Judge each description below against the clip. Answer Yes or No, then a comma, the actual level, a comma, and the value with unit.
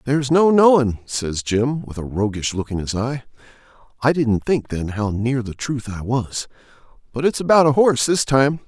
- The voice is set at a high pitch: No, low, 125 Hz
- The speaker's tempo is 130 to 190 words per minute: No, average, 200 wpm